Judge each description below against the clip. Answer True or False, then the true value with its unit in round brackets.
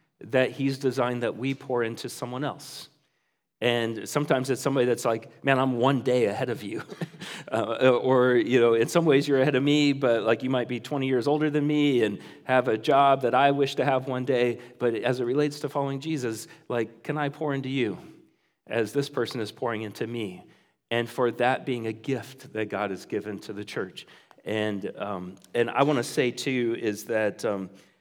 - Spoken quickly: True (210 wpm)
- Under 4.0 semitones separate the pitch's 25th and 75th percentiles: True (3.2 semitones)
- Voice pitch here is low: True (125 Hz)